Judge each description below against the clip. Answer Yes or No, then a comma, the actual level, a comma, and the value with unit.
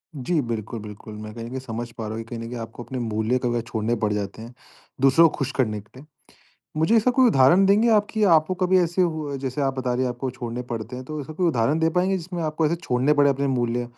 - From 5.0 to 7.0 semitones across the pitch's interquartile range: Yes, wide, 5.5 semitones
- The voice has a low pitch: Yes, low, 130 Hz